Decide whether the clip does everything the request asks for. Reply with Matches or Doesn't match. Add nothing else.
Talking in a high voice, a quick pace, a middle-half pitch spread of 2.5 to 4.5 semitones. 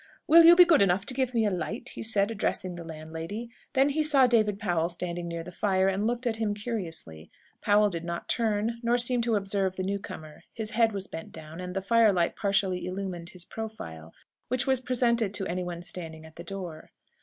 Doesn't match